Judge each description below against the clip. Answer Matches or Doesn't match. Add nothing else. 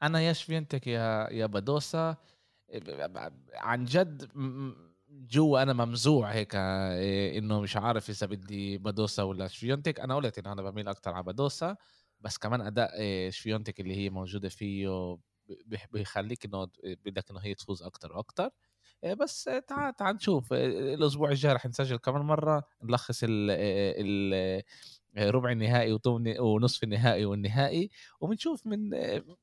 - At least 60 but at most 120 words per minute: Doesn't match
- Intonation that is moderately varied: Doesn't match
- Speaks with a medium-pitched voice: Doesn't match